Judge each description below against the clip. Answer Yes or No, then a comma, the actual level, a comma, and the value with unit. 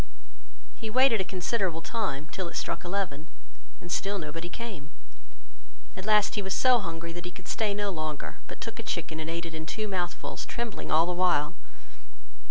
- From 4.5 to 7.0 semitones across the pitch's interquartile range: No, average, 3.8 semitones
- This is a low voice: No, medium, 180 Hz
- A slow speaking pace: No, average, 185 wpm